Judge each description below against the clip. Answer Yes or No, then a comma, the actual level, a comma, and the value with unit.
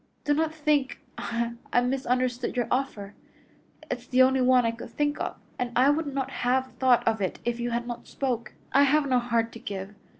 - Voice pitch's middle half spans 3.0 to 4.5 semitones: No, narrow, 2.4 semitones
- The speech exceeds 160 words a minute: Yes, average, 200 wpm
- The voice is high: Yes, very high, 250 Hz